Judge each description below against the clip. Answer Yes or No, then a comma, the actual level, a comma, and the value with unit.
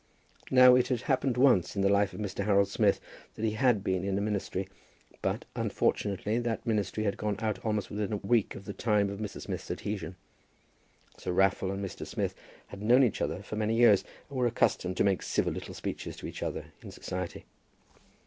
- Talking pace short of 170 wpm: No, fast, 205 wpm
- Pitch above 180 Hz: No, low, 105 Hz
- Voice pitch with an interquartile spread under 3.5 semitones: Yes, narrow, 2.6 semitones